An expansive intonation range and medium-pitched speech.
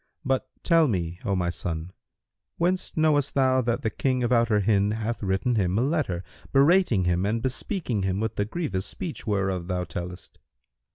No: wide, 6.1 semitones; low, 110 Hz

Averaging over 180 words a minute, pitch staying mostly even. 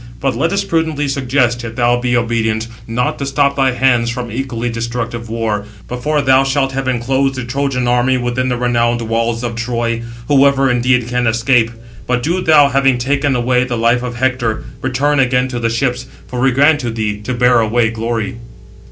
Yes: average, 190 wpm; narrow, 2.3 semitones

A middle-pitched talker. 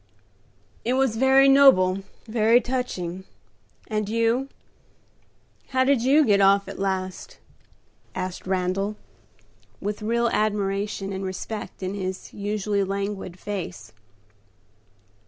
No: high, 205 Hz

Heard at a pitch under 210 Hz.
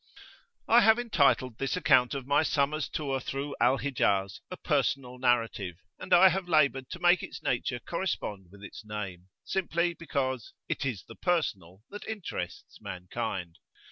Yes: low, 135 Hz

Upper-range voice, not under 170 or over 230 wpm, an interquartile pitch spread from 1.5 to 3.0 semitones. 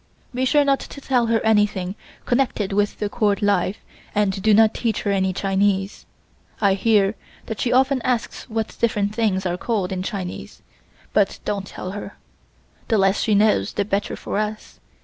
Yes: high, 210 Hz; average, 175 wpm; narrow, 2.5 semitones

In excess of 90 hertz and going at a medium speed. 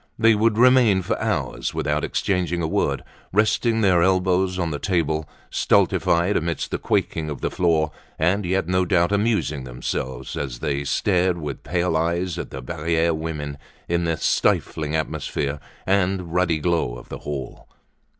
No: very low, 85 Hz; average, 160 wpm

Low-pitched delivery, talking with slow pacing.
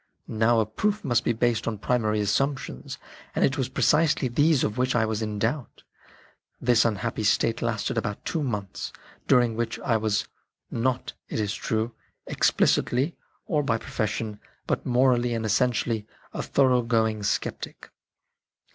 No: low, 115 Hz; average, 150 wpm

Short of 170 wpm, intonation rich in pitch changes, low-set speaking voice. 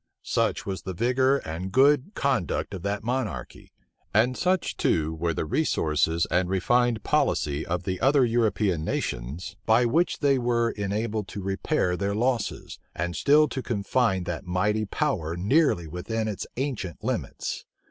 Yes: average, 150 wpm; wide, 6.0 semitones; low, 105 Hz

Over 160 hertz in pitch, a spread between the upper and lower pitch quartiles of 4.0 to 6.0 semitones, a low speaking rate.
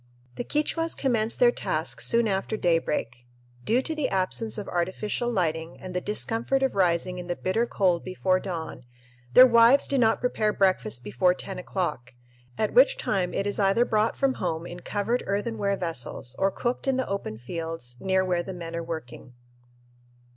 No: high, 190 Hz; average, 5.2 semitones; average, 175 wpm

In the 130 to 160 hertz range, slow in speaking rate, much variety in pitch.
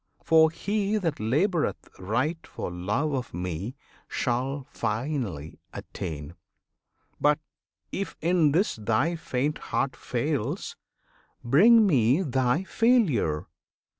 Yes: medium, 140 Hz; slow, 105 wpm; wide, 7.4 semitones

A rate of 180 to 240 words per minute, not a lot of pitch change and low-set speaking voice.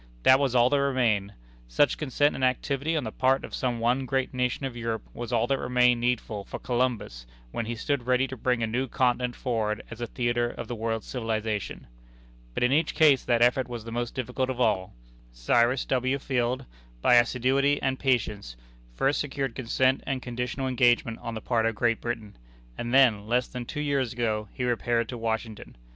Yes: average, 195 wpm; narrow, 2.2 semitones; low, 125 Hz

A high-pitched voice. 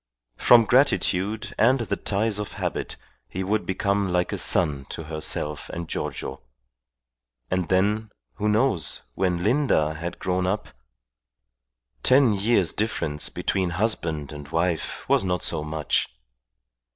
No: very low, 95 Hz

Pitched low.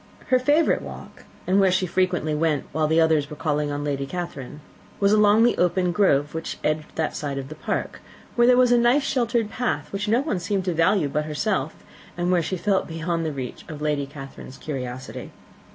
No: medium, 165 Hz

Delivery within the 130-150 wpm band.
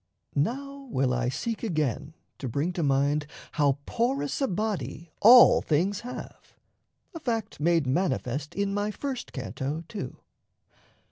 Yes: slow, 135 wpm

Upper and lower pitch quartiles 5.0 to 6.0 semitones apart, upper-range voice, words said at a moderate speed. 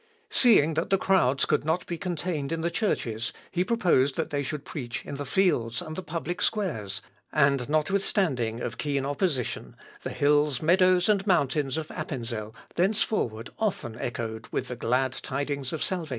No: wide, 5.6 semitones; medium, 150 Hz; average, 165 wpm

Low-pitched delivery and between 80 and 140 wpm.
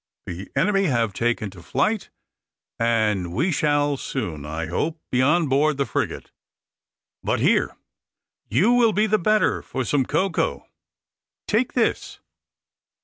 No: medium, 145 Hz; slow, 135 wpm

